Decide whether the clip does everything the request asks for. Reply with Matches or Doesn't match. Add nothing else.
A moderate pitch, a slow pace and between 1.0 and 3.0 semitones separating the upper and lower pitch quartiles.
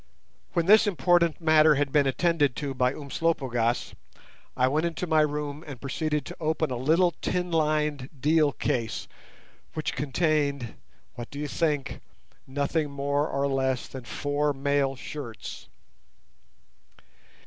Matches